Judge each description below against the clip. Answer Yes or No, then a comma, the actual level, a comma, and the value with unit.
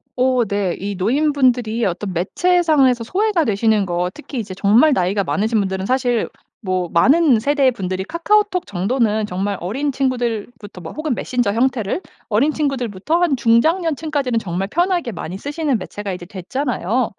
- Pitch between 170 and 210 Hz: No, high, 235 Hz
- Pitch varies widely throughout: Yes, wide, 6.3 semitones